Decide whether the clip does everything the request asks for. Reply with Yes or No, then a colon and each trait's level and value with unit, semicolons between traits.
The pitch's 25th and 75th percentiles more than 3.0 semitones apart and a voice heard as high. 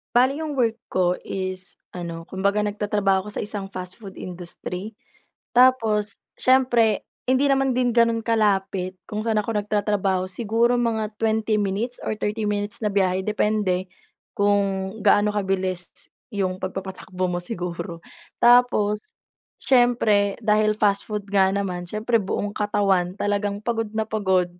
No: average, 2.7 semitones; high, 205 Hz